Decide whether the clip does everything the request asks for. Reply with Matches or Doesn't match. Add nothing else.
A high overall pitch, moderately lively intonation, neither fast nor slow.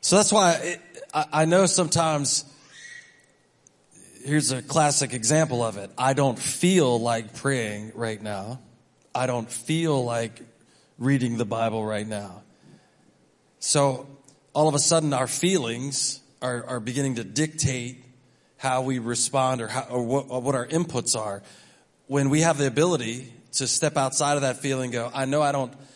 Doesn't match